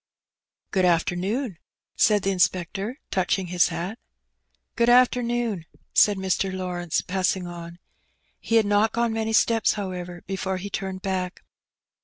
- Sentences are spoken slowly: Yes, slow, 130 wpm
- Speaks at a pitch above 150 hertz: Yes, high, 190 Hz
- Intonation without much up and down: No, average, 3.5 semitones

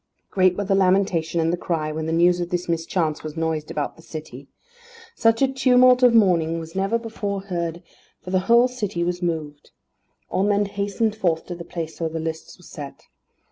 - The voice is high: No, medium, 175 Hz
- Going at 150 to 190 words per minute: No, average, 200 wpm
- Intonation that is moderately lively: Yes, average, 3.7 semitones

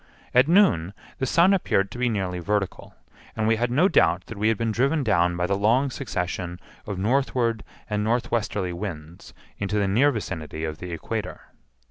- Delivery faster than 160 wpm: Yes, average, 180 wpm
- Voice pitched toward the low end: Yes, low, 105 Hz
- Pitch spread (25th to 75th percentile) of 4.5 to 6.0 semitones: Yes, average, 5.3 semitones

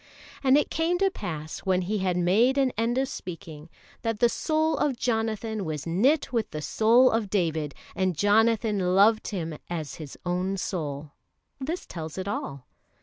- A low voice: No, high, 200 Hz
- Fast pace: No, average, 170 wpm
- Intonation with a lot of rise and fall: Yes, wide, 5.7 semitones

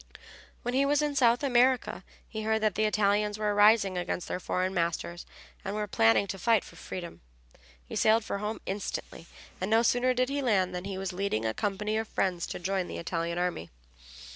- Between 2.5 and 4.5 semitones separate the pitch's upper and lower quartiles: Yes, average, 3.7 semitones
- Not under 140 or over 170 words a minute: No, average, 200 wpm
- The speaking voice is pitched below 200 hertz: No, high, 205 Hz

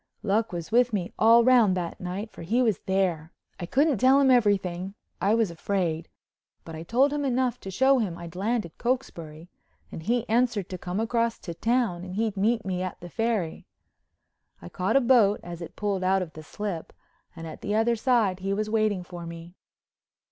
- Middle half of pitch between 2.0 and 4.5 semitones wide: No, average, 4.9 semitones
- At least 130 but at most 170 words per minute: No, average, 190 wpm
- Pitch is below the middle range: No, high, 200 Hz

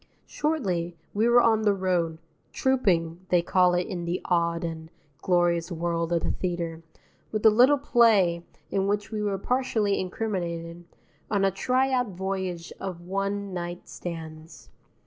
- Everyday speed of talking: Yes, average, 150 wpm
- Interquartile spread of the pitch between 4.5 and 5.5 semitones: No, average, 3.5 semitones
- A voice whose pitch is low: No, medium, 185 Hz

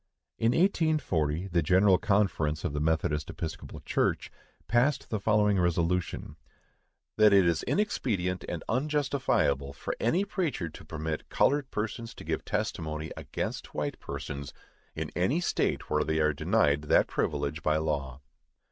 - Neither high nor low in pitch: No, very low, 90 Hz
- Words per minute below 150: Yes, average, 140 wpm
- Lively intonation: Yes, wide, 7.1 semitones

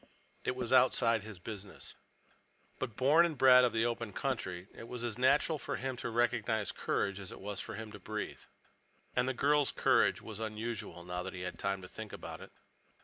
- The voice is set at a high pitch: No, low, 115 Hz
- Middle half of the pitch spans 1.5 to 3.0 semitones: No, average, 4.0 semitones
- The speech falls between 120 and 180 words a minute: No, fast, 205 wpm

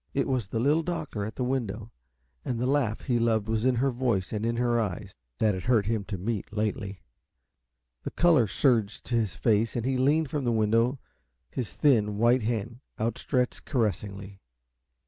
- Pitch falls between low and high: No, low, 115 Hz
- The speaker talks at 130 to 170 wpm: No, average, 185 wpm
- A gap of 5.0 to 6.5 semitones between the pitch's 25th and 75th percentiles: No, average, 3.2 semitones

